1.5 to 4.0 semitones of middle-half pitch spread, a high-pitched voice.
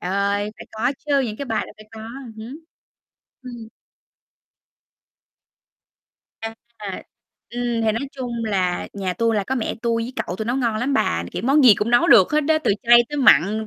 Yes: average, 3.4 semitones; high, 230 Hz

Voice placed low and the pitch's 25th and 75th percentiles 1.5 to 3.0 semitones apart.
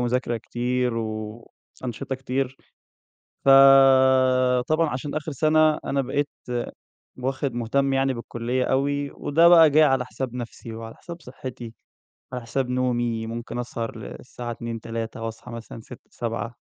Yes: low, 125 Hz; narrow, 2.6 semitones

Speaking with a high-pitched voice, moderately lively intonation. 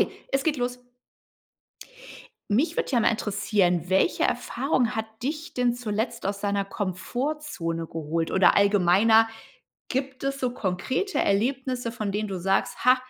Yes: high, 225 Hz; average, 4.6 semitones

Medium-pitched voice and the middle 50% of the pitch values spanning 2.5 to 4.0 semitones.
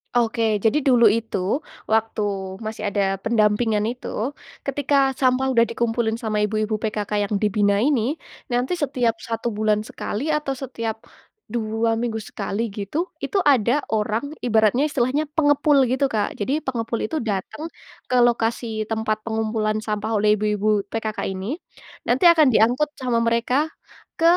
No: high, 225 Hz; average, 2.9 semitones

